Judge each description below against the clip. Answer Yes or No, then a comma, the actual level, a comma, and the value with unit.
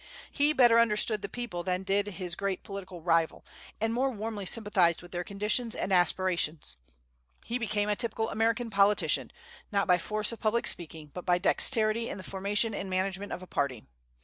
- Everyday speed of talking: Yes, average, 180 wpm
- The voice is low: No, high, 200 Hz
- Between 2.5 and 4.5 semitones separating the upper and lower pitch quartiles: Yes, average, 3.6 semitones